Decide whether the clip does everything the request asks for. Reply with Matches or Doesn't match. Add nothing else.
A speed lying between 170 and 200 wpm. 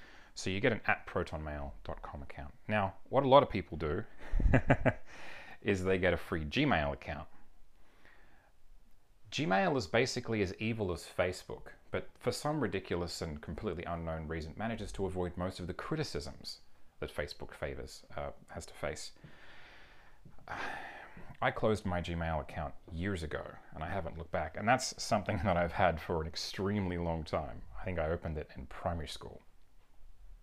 Doesn't match